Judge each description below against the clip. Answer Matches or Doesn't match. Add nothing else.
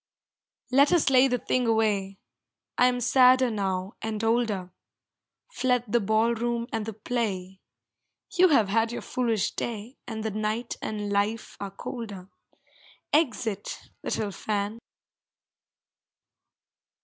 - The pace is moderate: Doesn't match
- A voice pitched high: Matches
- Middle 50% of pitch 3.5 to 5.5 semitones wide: Doesn't match